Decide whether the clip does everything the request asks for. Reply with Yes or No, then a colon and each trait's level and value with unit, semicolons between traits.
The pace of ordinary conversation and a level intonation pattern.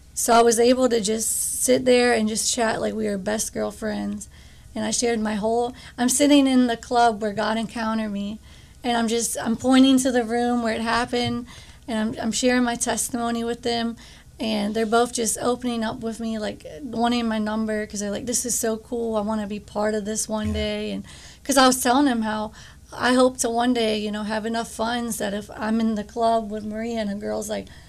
No: fast, 230 wpm; narrow, 1.9 semitones